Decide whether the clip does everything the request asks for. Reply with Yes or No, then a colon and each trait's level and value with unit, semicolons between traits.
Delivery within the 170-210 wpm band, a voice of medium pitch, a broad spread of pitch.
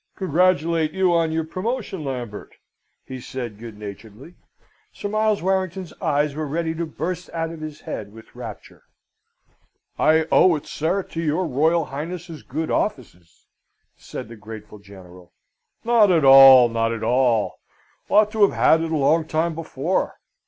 No: average, 155 wpm; medium, 155 Hz; wide, 6.0 semitones